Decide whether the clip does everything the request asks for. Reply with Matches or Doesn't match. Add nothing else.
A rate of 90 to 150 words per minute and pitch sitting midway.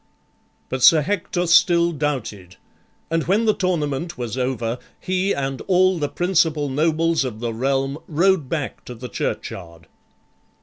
Matches